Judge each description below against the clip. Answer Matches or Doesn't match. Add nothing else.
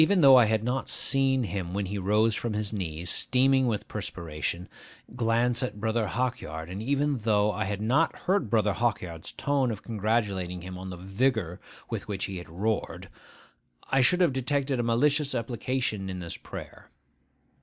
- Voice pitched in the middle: Doesn't match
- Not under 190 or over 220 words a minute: Doesn't match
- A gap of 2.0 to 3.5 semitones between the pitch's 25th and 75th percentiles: Doesn't match